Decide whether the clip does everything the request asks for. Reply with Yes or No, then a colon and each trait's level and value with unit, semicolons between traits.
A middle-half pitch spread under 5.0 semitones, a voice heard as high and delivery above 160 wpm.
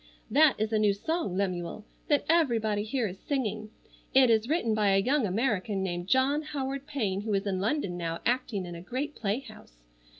No: wide, 5.5 semitones; high, 215 Hz; average, 190 wpm